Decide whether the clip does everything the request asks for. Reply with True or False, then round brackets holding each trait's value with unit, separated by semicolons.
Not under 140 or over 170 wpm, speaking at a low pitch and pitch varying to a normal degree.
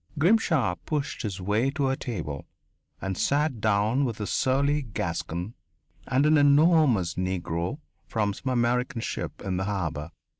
False (145 wpm; 115 Hz; 6.8 semitones)